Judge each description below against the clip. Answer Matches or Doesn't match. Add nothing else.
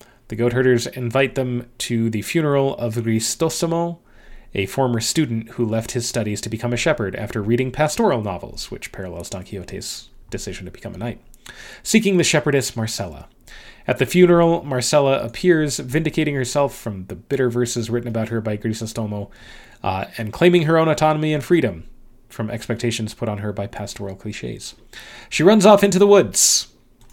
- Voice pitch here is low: Matches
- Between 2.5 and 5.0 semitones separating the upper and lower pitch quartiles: Doesn't match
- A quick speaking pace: Doesn't match